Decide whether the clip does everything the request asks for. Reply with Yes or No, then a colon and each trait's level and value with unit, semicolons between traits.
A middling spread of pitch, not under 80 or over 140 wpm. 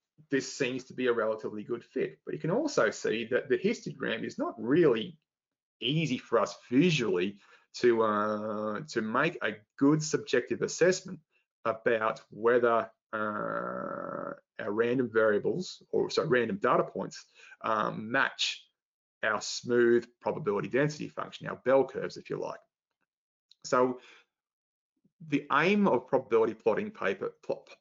No: wide, 7.6 semitones; slow, 135 wpm